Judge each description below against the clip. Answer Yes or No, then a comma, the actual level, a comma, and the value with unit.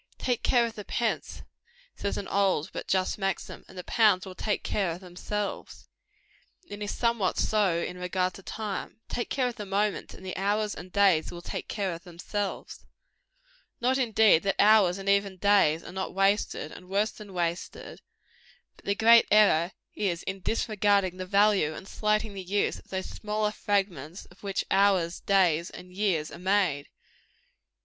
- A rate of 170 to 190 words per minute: Yes, average, 175 wpm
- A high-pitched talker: Yes, high, 195 Hz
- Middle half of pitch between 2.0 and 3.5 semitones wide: Yes, narrow, 2.4 semitones